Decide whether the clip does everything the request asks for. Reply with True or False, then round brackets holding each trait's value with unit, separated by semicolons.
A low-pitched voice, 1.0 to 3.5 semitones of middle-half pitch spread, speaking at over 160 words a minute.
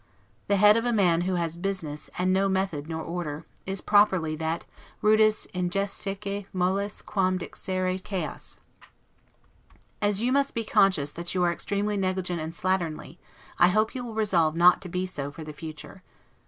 False (185 Hz; 3.0 semitones; 170 wpm)